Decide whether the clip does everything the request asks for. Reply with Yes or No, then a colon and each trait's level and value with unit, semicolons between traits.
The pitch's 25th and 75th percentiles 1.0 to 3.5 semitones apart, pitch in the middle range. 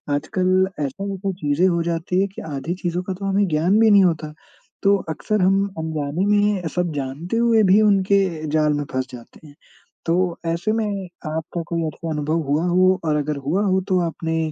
No: average, 4.1 semitones; medium, 175 Hz